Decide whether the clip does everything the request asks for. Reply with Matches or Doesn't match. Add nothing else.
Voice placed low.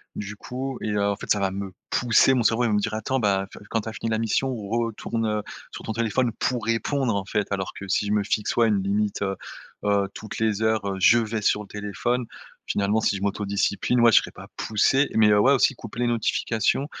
Matches